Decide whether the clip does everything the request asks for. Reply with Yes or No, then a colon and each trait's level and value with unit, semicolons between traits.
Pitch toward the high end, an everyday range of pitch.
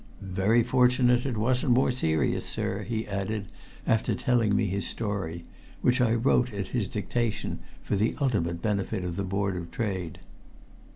No: low, 105 Hz; average, 4.0 semitones